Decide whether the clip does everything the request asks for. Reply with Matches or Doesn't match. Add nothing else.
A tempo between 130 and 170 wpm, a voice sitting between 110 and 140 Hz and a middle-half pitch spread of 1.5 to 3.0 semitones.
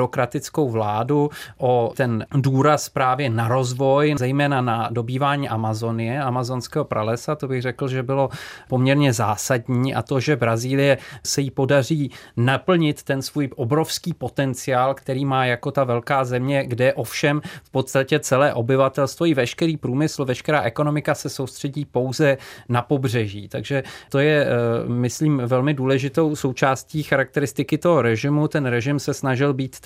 Matches